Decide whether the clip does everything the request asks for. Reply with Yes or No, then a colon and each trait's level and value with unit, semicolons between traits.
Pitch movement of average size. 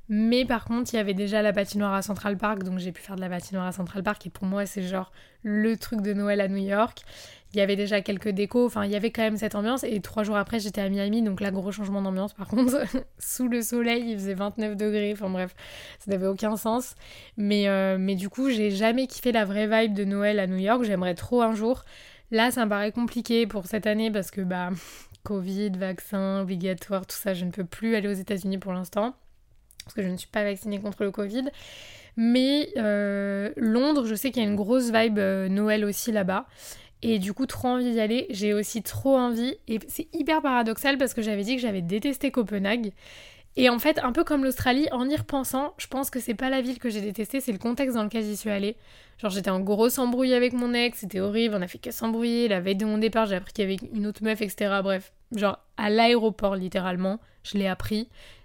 Yes: average, 3.0 semitones